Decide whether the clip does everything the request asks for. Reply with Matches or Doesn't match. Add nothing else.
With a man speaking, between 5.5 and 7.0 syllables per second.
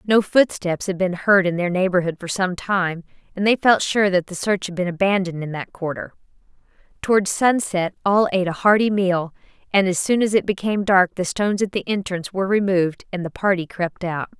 Doesn't match